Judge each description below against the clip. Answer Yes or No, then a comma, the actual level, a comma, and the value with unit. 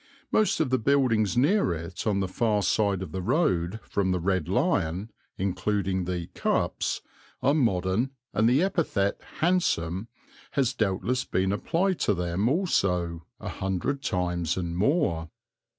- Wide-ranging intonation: Yes, wide, 6.3 semitones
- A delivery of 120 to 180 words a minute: Yes, average, 145 wpm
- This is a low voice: Yes, low, 100 Hz